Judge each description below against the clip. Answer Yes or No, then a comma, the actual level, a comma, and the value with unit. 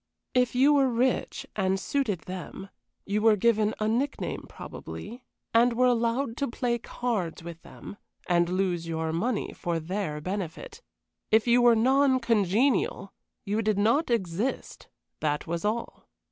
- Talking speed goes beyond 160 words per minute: No, average, 145 wpm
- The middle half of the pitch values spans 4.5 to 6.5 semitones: Yes, average, 4.9 semitones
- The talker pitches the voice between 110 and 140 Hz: No, high, 220 Hz